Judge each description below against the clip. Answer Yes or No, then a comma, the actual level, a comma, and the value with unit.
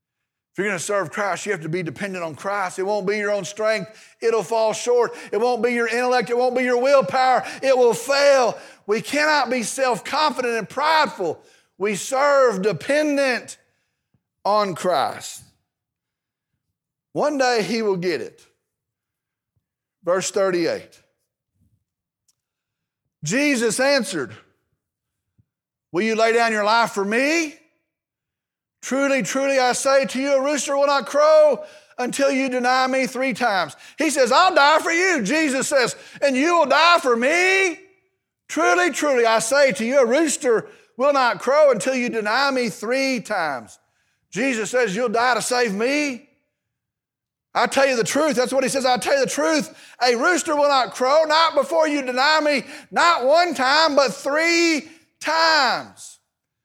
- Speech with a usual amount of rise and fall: Yes, average, 4.5 semitones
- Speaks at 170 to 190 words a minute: No, average, 160 wpm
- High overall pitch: Yes, very high, 260 Hz